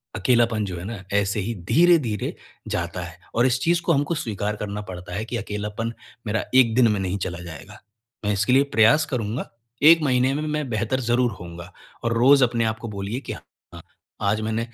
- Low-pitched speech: Yes, low, 115 Hz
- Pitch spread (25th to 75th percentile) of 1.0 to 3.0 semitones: No, average, 3.7 semitones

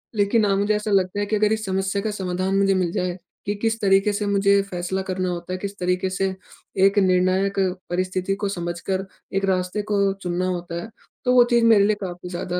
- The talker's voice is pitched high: Yes, high, 195 Hz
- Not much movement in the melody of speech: Yes, narrow, 1.9 semitones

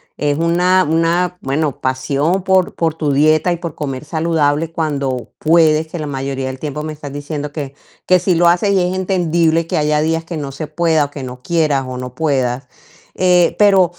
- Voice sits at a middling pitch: Yes, medium, 155 Hz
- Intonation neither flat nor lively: Yes, average, 3.1 semitones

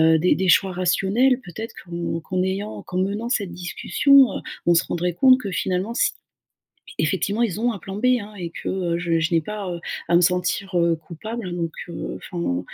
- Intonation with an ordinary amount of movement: Yes, average, 3.6 semitones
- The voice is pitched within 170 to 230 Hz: Yes, medium, 185 Hz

